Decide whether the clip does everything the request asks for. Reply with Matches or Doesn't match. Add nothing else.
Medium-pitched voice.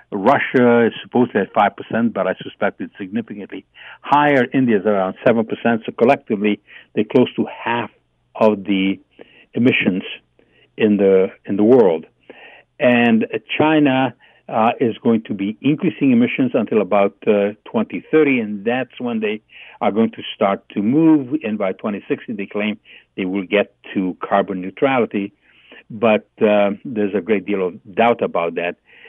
Doesn't match